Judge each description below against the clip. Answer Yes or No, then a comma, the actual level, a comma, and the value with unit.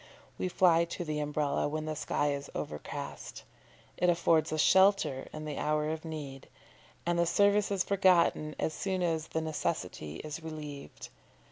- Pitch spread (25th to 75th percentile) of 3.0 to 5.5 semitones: No, narrow, 2.5 semitones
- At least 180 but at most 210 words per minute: No, average, 160 wpm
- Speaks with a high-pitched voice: No, medium, 155 Hz